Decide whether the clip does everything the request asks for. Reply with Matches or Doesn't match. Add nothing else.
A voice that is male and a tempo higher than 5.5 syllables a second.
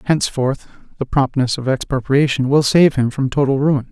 Doesn't match